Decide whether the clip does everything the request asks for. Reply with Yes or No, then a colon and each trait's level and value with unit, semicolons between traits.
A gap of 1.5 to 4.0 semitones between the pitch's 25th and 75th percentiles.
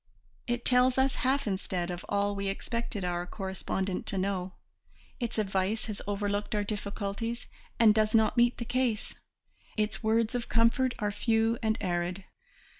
Yes: average, 2.9 semitones